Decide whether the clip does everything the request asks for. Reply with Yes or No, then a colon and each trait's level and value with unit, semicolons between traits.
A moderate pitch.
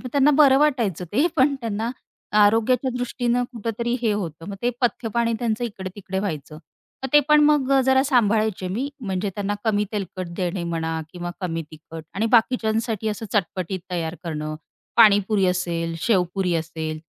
No: high, 205 Hz